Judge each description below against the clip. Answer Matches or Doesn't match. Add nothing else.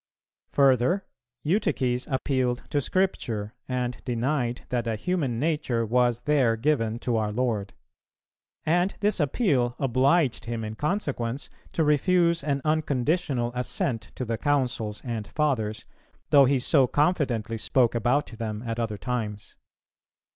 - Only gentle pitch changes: Doesn't match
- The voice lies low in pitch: Matches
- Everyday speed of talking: Doesn't match